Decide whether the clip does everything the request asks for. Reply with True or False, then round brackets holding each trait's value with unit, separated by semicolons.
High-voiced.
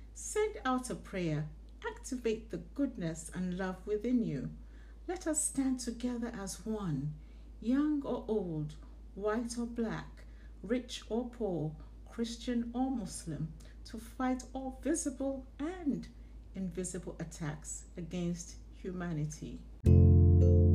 True (215 Hz)